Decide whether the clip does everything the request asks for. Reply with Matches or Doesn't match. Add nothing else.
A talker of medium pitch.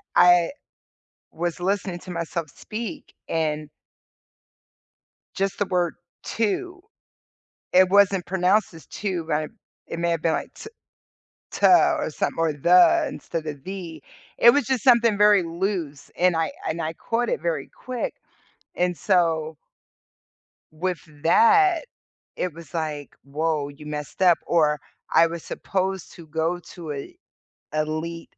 Matches